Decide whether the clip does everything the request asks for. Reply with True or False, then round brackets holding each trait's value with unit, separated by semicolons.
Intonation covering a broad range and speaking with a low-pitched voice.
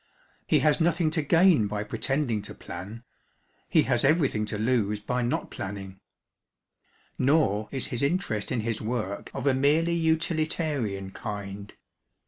True (6.8 semitones; 125 Hz)